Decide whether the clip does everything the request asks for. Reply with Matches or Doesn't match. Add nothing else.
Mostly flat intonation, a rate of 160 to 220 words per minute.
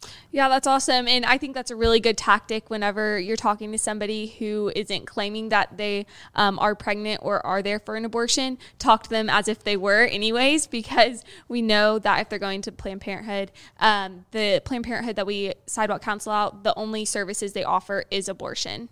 Matches